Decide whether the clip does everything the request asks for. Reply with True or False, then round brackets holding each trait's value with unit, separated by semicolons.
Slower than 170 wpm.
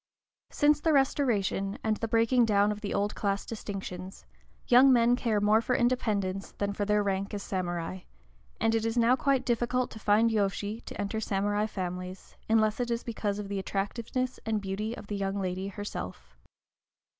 False (180 wpm)